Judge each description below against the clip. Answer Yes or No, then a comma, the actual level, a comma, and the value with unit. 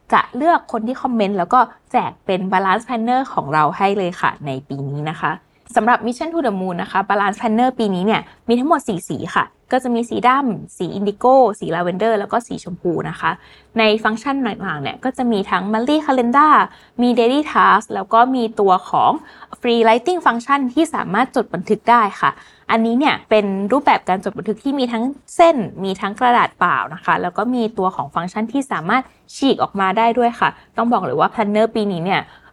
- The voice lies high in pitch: Yes, high, 225 Hz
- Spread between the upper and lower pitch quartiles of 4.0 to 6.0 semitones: Yes, average, 4.6 semitones